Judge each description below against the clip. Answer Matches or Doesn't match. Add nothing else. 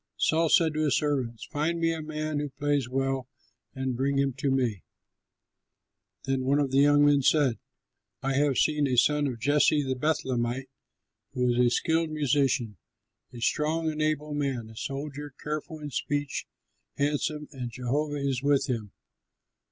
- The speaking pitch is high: Doesn't match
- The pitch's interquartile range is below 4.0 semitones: Matches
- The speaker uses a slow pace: Doesn't match